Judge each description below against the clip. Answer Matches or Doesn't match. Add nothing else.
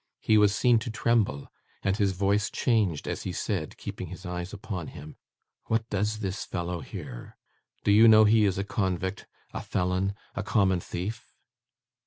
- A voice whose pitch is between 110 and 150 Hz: Doesn't match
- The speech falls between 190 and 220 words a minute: Doesn't match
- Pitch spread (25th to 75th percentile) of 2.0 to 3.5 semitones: Matches